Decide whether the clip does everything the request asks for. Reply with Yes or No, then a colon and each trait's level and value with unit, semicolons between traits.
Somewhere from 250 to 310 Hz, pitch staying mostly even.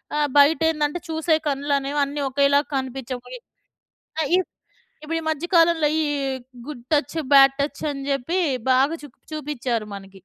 Yes: very high, 285 Hz; narrow, 2.3 semitones